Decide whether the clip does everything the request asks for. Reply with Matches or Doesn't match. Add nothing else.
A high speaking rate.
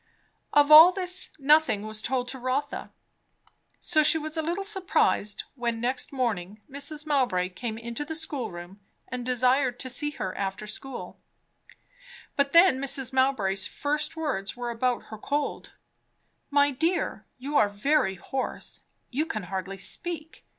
Doesn't match